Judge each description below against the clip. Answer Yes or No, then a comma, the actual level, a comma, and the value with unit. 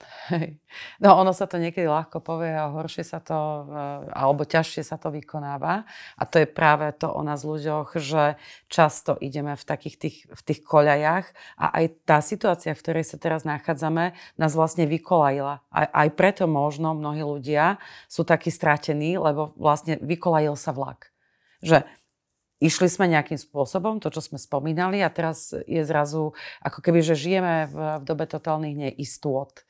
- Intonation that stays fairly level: Yes, narrow, 1.8 semitones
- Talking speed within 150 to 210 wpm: Yes, average, 160 wpm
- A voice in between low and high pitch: Yes, medium, 155 Hz